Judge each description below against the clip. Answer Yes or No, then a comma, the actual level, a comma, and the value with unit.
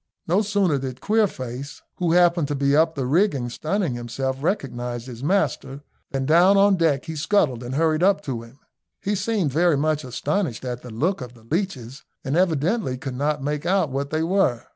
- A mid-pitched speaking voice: Yes, medium, 150 Hz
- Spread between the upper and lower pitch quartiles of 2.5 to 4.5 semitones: No, wide, 5.5 semitones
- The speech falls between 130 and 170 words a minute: No, average, 190 wpm